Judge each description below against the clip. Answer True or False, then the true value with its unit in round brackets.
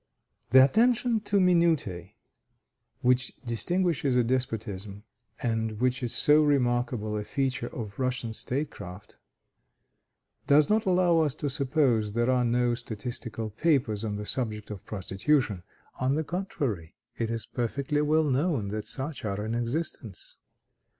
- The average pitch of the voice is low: True (125 Hz)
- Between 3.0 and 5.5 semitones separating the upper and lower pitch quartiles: True (5.2 semitones)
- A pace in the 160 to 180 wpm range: False (135 wpm)